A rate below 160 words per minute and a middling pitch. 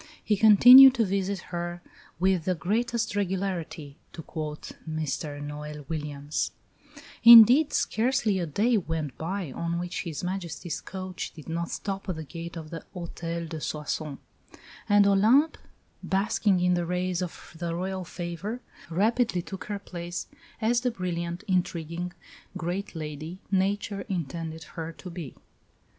Yes: average, 140 wpm; medium, 180 Hz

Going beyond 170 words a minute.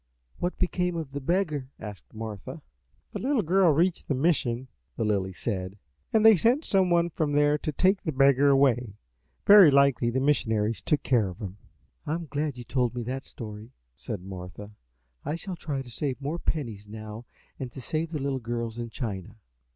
Yes: average, 190 wpm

